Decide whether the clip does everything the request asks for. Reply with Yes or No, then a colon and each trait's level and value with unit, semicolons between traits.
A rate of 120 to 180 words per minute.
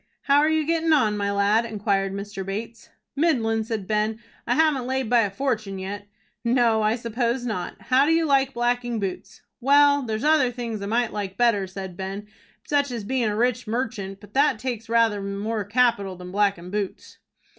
No: average, 190 wpm